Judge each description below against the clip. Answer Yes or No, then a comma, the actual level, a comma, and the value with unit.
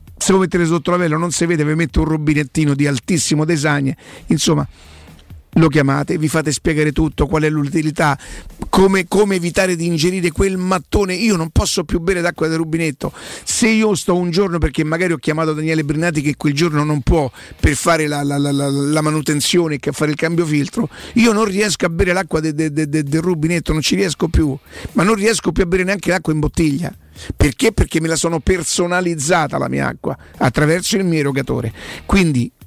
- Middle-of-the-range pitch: Yes, medium, 160 Hz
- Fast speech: Yes, fast, 200 wpm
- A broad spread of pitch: No, average, 3.1 semitones